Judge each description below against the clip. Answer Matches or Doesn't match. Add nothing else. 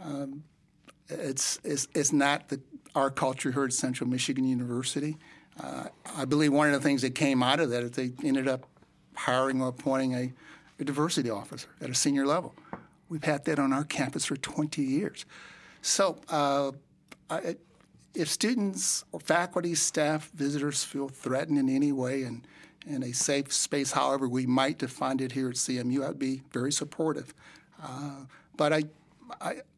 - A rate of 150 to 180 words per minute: Matches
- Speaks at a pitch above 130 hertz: Matches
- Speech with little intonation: Matches